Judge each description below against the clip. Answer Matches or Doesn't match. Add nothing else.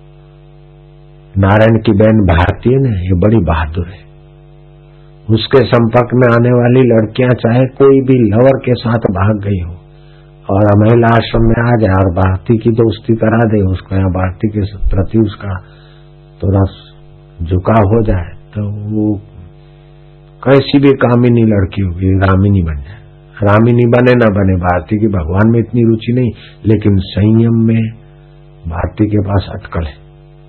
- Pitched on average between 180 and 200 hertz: Doesn't match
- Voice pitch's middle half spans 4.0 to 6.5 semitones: Matches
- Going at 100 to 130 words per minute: Doesn't match